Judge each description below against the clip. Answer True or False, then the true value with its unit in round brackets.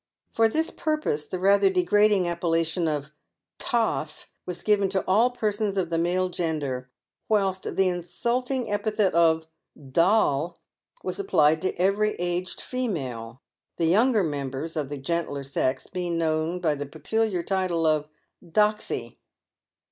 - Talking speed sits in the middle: True (150 wpm)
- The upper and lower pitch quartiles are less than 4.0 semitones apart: False (4.8 semitones)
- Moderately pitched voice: True (175 Hz)